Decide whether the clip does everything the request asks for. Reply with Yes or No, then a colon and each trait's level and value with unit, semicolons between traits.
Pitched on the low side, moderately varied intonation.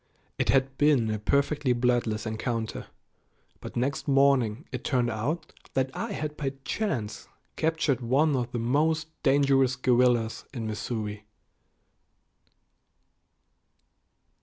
Yes: low, 130 Hz; average, 3.5 semitones